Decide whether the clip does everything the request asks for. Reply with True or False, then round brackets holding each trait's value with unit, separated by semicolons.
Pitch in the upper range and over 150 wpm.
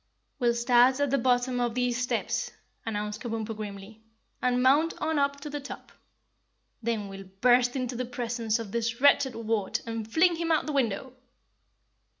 True (245 Hz; 170 wpm)